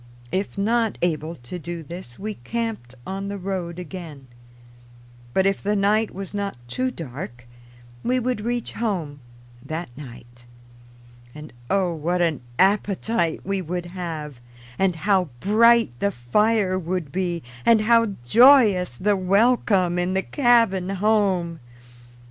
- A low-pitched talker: No, high, 190 Hz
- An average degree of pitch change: Yes, average, 4.0 semitones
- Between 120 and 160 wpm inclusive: Yes, slow, 135 wpm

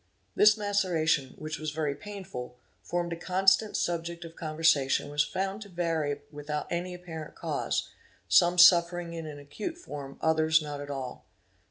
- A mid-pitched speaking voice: Yes, medium, 165 Hz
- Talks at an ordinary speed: Yes, average, 160 wpm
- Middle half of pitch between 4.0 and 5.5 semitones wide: No, average, 3.1 semitones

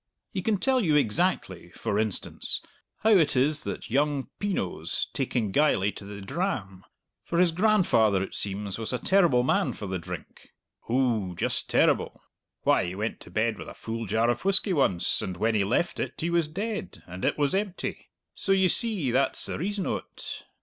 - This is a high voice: No, low, 130 Hz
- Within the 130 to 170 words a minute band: No, average, 190 wpm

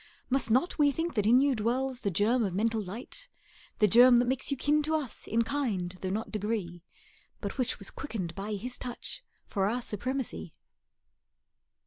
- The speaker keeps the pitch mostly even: No, average, 4.3 semitones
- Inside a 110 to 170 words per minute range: No, average, 180 wpm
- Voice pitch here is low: No, high, 230 Hz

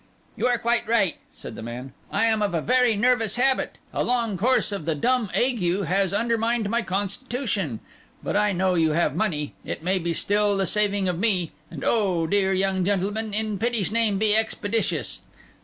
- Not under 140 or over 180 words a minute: No, average, 190 wpm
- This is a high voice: Yes, high, 205 Hz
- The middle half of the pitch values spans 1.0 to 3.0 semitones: No, average, 3.6 semitones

